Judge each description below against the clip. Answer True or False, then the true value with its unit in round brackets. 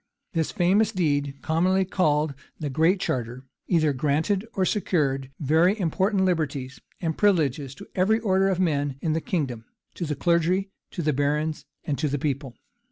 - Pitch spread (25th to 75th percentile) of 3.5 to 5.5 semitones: True (4.6 semitones)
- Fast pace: False (165 wpm)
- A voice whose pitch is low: False (160 Hz)